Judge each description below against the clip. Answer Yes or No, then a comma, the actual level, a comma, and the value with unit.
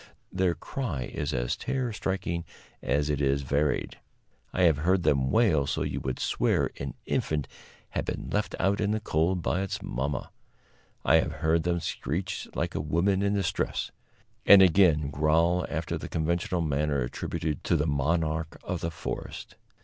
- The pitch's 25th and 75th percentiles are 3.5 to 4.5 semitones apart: Yes, average, 4.0 semitones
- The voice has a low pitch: Yes, very low, 80 Hz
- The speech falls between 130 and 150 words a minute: No, average, 165 wpm